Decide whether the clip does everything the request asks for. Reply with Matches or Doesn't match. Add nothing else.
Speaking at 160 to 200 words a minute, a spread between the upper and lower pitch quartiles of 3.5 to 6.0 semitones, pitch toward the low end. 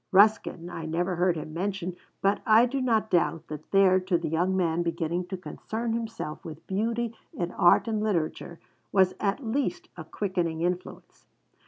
Doesn't match